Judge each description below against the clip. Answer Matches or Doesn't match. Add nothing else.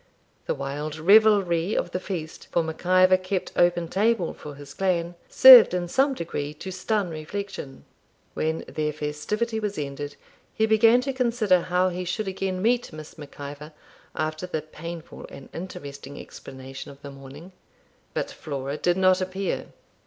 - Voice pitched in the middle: Matches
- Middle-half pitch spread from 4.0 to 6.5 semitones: Matches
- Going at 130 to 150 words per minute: Doesn't match